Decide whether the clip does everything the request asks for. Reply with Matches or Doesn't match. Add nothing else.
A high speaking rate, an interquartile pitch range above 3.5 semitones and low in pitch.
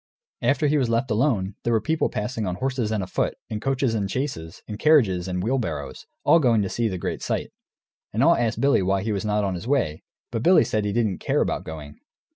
Matches